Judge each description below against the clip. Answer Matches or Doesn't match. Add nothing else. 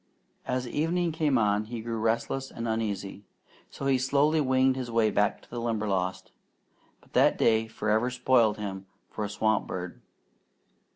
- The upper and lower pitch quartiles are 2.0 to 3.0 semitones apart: Doesn't match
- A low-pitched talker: Matches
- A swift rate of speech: Doesn't match